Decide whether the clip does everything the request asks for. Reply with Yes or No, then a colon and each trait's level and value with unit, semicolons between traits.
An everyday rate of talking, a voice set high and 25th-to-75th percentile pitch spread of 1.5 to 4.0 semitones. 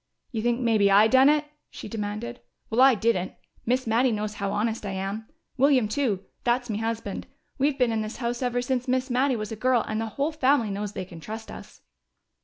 No: fast, 210 wpm; high, 230 Hz; average, 3.2 semitones